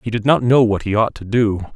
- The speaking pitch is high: No, low, 110 Hz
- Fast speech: Yes, fast, 305 wpm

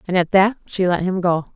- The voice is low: No, medium, 185 Hz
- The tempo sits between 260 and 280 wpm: Yes, fast, 270 wpm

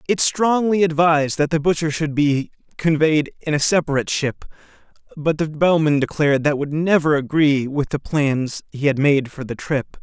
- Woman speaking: No, male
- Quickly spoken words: No, average, 180 wpm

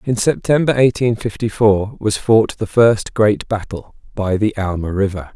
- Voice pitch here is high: No, low, 105 Hz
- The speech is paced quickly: No, average, 170 wpm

